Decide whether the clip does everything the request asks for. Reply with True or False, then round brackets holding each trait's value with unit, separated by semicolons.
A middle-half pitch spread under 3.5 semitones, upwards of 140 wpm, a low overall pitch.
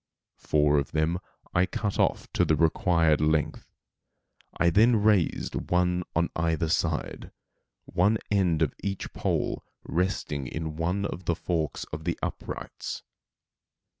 False (2.8 semitones; 135 wpm; 85 Hz)